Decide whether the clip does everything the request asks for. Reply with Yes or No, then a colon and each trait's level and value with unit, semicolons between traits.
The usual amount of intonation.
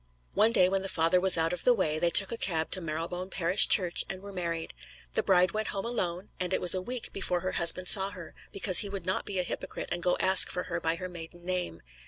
No: narrow, 2.0 semitones